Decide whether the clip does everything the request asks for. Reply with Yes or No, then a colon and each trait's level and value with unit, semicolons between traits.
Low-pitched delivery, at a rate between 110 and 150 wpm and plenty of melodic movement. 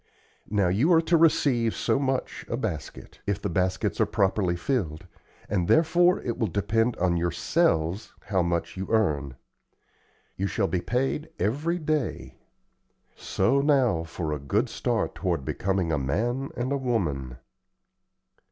Yes: low, 100 Hz; average, 145 wpm; wide, 7.6 semitones